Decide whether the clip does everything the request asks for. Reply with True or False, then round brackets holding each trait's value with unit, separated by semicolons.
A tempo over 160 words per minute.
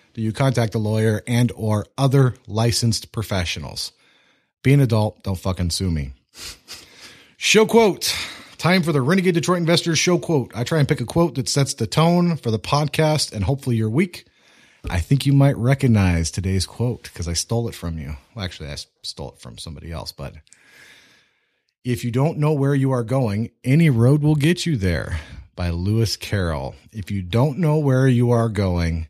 True (185 wpm)